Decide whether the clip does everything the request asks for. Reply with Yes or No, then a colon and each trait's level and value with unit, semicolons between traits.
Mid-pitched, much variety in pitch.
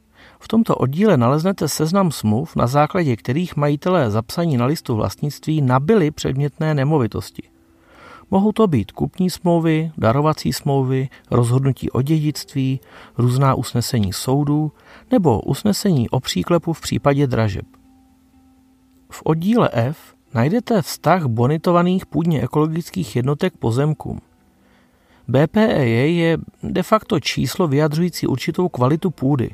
Yes: medium, 150 Hz; wide, 6.2 semitones